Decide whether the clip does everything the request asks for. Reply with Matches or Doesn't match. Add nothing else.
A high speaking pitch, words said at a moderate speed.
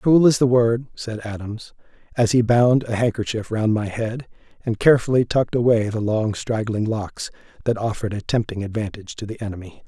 Doesn't match